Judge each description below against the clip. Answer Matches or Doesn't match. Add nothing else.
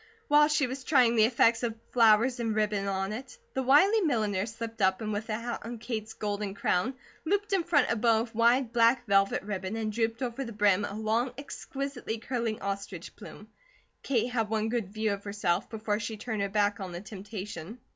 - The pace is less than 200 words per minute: Doesn't match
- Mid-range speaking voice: Doesn't match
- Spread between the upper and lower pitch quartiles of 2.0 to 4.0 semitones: Matches